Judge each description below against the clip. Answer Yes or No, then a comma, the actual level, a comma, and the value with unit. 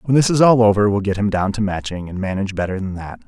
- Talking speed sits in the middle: No, fast, 295 wpm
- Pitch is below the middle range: Yes, low, 105 Hz